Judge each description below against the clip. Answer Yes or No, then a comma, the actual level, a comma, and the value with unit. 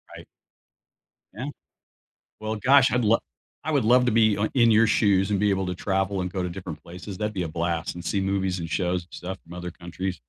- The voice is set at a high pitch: No, very low, 95 Hz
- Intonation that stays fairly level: No, average, 3.4 semitones